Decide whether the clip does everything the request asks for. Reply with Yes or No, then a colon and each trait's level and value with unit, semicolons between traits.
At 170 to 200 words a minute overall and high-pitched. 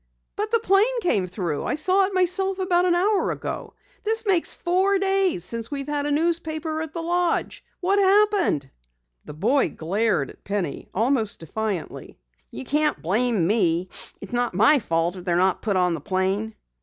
Yes: average, 175 wpm; very high, 285 Hz